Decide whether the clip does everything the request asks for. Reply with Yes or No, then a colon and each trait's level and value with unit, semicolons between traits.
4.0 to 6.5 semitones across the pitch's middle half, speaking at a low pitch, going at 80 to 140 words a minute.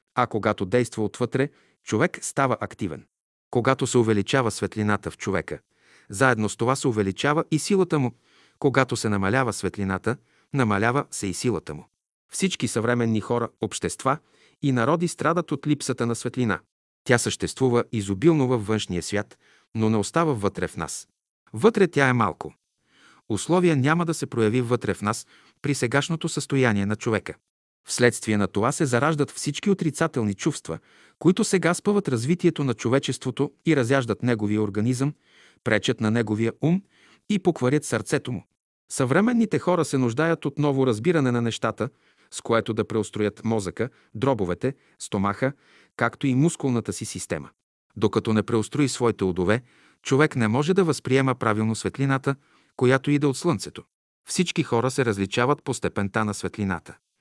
No: average, 5.1 semitones; low, 125 Hz; average, 150 wpm